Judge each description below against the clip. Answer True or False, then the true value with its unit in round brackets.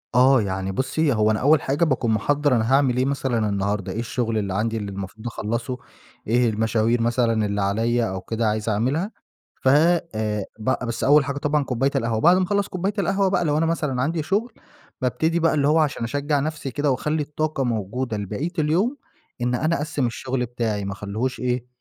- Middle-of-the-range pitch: False (125 Hz)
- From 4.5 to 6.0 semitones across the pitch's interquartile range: True (5.2 semitones)